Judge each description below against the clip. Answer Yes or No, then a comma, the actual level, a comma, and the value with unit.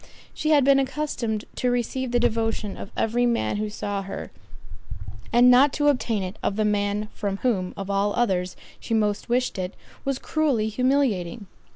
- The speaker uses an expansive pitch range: No, average, 3.8 semitones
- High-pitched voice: Yes, high, 225 Hz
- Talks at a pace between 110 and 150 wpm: No, average, 175 wpm